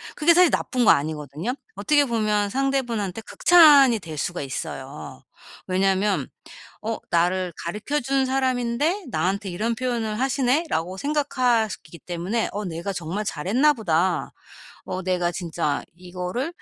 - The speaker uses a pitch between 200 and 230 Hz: Yes, high, 210 Hz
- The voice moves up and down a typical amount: No, wide, 6.6 semitones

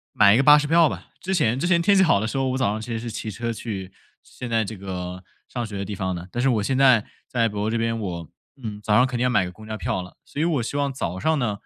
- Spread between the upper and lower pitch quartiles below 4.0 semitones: No, average, 4.6 semitones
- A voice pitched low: Yes, low, 115 Hz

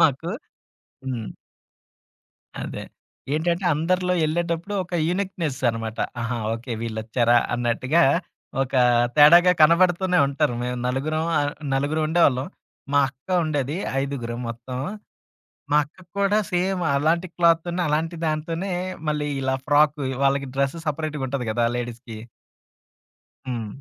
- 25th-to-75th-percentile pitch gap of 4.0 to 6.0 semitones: Yes, average, 4.9 semitones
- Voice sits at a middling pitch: Yes, medium, 150 Hz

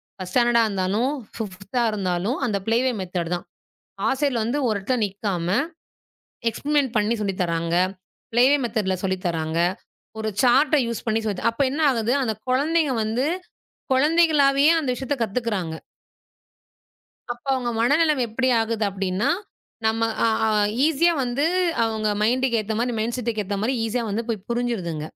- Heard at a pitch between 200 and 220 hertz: No, high, 230 Hz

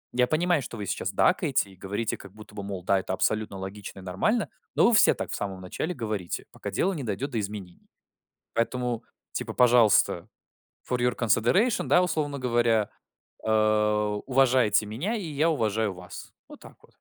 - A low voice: Yes, low, 110 Hz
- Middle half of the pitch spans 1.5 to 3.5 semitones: No, average, 4.3 semitones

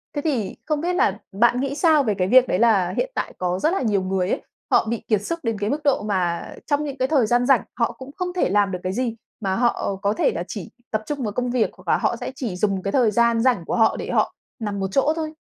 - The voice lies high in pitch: Yes, high, 230 Hz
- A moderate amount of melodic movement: No, wide, 5.7 semitones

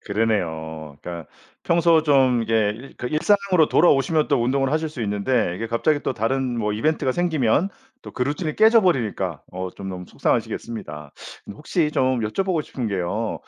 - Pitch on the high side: No, low, 125 Hz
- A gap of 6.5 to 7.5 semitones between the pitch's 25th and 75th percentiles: Yes, wide, 6.9 semitones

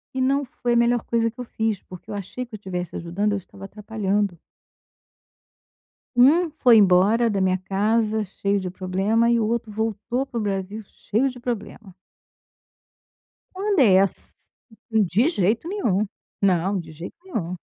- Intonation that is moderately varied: Yes, average, 3.6 semitones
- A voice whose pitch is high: Yes, high, 210 Hz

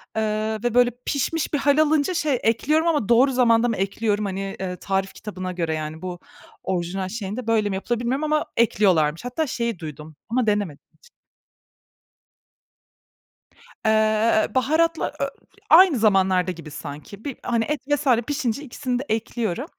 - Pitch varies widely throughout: Yes, wide, 5.8 semitones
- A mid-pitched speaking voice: No, high, 225 Hz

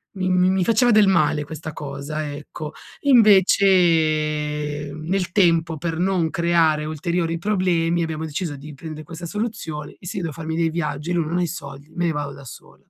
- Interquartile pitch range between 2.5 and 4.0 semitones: Yes, average, 2.9 semitones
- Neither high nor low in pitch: Yes, medium, 165 Hz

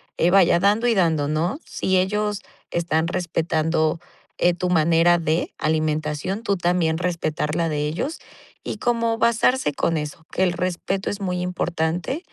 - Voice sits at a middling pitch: Yes, medium, 175 Hz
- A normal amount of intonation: Yes, average, 3.1 semitones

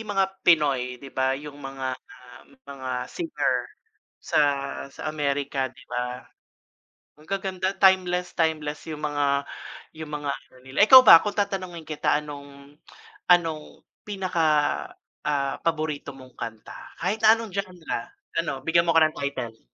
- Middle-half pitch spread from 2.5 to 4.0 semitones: No, average, 4.6 semitones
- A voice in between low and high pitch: Yes, medium, 150 Hz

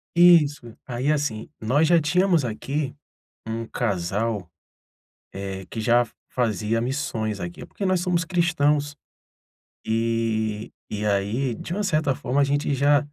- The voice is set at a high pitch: No, low, 125 Hz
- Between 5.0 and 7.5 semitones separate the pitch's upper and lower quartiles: Yes, wide, 5.5 semitones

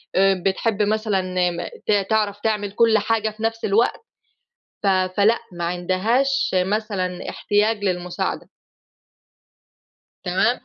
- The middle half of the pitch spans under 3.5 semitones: Yes, average, 2.9 semitones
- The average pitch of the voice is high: Yes, high, 205 Hz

